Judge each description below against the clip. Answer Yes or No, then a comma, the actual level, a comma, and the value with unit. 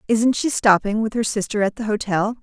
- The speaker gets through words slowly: No, fast, 225 wpm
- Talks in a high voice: Yes, high, 215 Hz